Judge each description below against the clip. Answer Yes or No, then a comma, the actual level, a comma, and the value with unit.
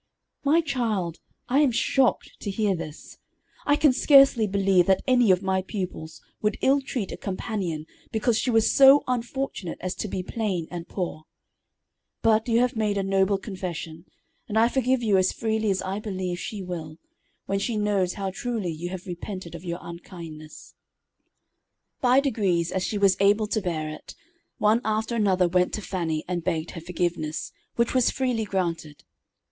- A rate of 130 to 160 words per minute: No, average, 175 wpm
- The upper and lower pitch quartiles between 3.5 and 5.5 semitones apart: Yes, average, 4.3 semitones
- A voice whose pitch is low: No, high, 195 Hz